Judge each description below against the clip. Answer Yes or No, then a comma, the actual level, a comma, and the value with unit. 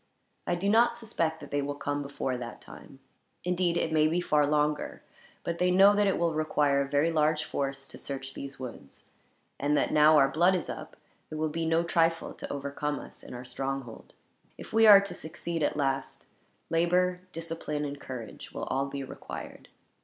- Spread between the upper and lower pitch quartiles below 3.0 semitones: No, average, 3.6 semitones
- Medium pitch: Yes, medium, 150 Hz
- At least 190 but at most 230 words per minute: Yes, average, 195 wpm